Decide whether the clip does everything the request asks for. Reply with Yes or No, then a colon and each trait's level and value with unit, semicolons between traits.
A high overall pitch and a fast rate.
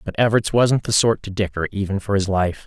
No: low, 100 Hz; fast, 250 wpm